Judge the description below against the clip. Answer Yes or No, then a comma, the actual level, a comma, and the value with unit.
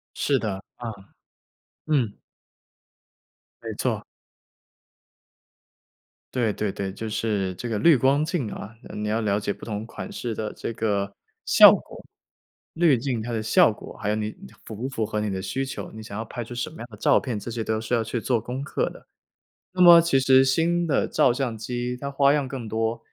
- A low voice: Yes, low, 115 Hz